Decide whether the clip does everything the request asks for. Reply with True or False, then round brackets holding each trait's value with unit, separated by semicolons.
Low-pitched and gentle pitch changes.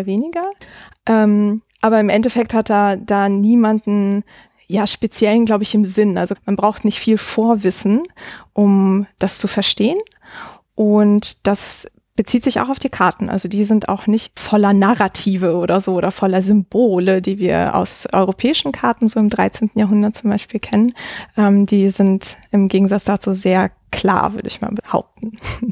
False (210 Hz; 1.9 semitones)